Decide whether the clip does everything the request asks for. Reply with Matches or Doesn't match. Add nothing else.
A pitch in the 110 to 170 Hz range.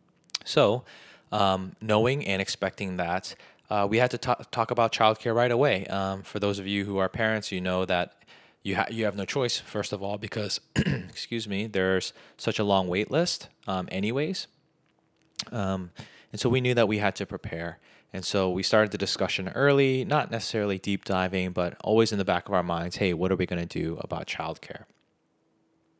Doesn't match